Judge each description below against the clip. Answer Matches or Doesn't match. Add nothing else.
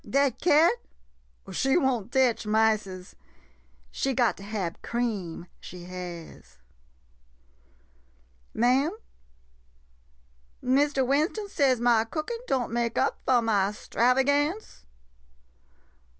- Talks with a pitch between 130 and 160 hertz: Doesn't match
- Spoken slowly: Matches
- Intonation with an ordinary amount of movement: Matches